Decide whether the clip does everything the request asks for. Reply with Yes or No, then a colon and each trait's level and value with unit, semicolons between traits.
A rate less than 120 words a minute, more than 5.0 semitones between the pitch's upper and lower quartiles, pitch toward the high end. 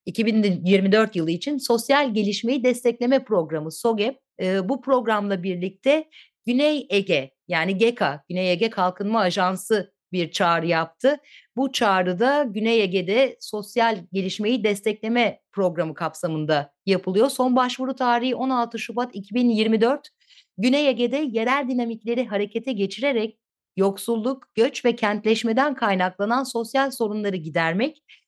No: average, 110 wpm; average, 4.7 semitones; high, 225 Hz